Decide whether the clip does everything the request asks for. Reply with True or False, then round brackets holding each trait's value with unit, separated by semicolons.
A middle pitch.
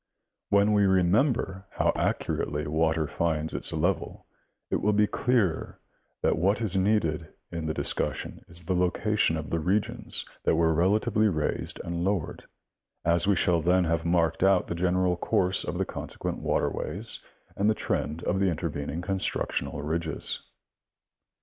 False (90 Hz)